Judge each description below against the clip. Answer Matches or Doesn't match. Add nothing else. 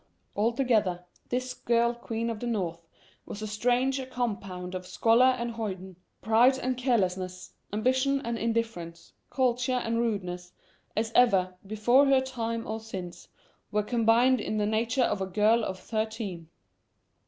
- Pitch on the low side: Doesn't match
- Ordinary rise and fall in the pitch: Matches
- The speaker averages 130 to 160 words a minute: Matches